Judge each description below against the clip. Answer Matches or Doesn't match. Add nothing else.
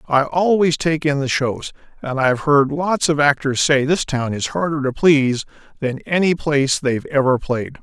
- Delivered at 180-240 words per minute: Matches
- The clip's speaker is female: Doesn't match